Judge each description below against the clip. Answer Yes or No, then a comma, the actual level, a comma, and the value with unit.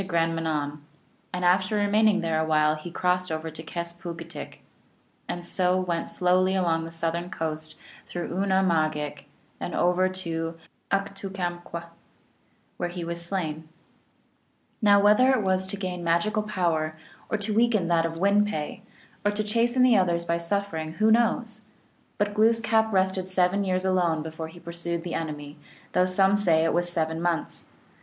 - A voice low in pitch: No, medium, 175 Hz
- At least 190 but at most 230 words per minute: No, average, 175 wpm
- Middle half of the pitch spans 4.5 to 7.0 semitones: No, average, 3.2 semitones